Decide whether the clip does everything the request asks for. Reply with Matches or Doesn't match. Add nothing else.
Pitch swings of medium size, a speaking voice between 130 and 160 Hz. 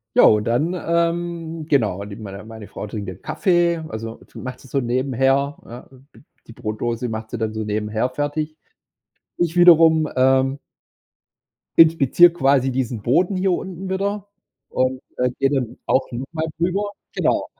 Doesn't match